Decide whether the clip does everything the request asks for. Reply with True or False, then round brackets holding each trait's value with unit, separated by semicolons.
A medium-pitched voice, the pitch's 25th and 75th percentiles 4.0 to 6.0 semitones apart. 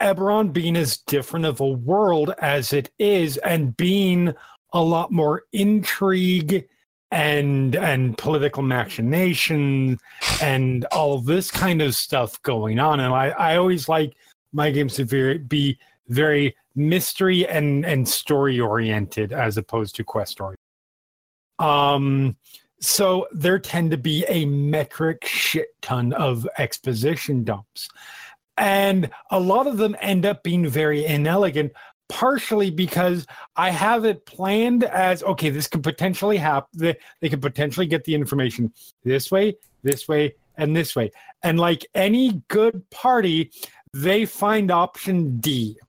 True (155 Hz; 5.2 semitones)